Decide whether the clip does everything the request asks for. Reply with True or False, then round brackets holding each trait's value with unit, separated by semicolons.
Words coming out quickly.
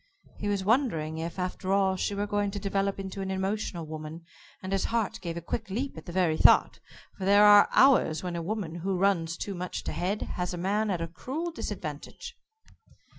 True (210 wpm)